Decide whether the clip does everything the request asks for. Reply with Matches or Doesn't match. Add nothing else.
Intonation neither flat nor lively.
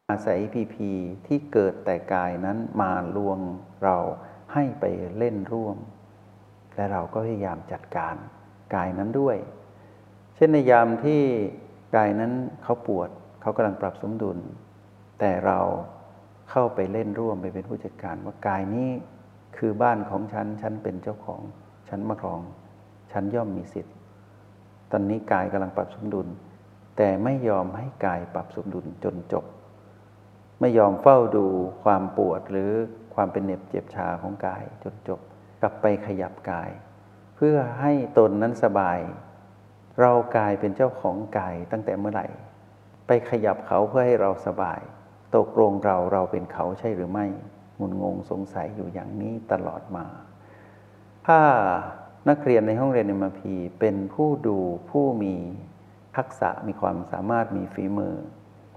Doesn't match